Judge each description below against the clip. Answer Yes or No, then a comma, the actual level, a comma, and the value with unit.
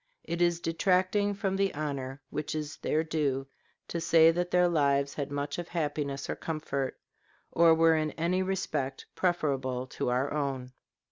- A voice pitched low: No, medium, 155 Hz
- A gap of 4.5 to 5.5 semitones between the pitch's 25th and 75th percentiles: No, average, 3.7 semitones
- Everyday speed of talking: Yes, average, 160 wpm